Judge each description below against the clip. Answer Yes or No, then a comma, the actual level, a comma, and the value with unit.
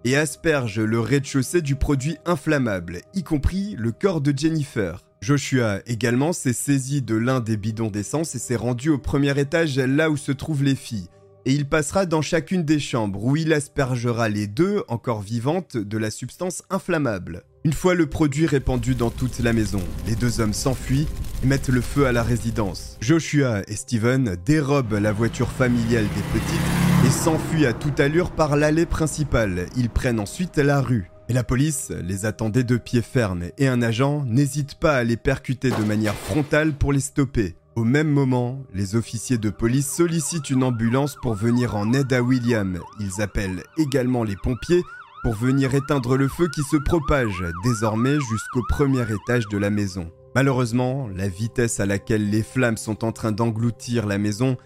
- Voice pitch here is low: Yes, low, 125 Hz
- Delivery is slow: No, average, 180 wpm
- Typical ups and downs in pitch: Yes, average, 4.6 semitones